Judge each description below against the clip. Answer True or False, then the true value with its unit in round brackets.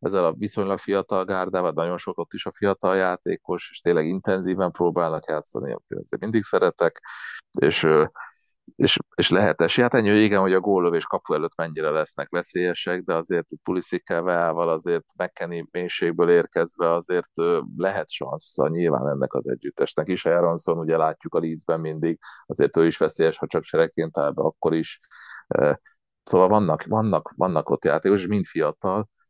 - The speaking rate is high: True (160 wpm)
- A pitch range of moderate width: True (4.1 semitones)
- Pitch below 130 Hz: True (95 Hz)